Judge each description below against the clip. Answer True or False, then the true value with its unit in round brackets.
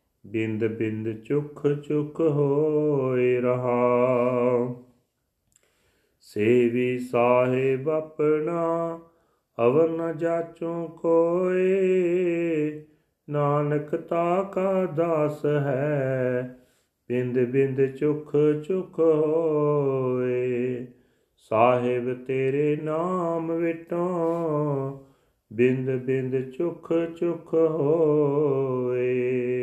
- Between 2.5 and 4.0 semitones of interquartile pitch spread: False (4.7 semitones)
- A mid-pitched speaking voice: True (145 Hz)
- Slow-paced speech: True (65 wpm)